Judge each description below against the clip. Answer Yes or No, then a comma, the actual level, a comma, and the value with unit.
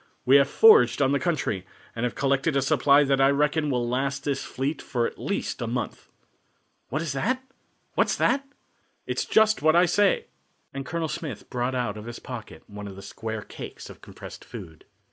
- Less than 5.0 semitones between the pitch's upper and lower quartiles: Yes, average, 4.3 semitones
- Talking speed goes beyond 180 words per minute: Yes, average, 190 wpm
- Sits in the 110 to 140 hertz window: Yes, low, 135 Hz